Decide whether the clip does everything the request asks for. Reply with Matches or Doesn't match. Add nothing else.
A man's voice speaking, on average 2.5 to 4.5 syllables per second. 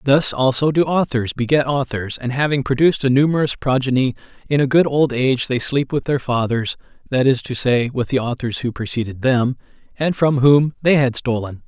Doesn't match